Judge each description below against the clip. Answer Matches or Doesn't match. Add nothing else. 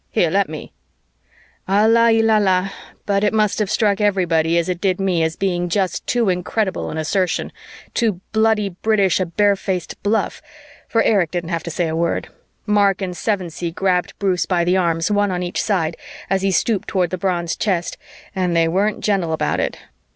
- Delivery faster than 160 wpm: Matches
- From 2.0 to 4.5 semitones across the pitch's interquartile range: Matches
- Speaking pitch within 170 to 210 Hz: Matches